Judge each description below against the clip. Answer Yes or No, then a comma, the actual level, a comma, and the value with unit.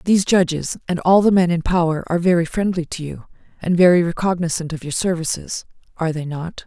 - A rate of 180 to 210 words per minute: Yes, average, 200 wpm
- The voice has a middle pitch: Yes, medium, 170 Hz